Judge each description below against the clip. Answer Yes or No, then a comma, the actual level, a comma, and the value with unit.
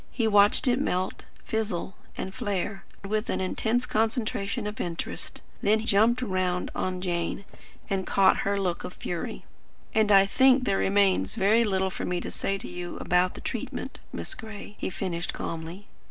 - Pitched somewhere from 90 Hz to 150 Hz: No, high, 195 Hz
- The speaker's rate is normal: Yes, average, 170 wpm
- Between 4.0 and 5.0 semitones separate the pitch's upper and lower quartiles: No, average, 3.0 semitones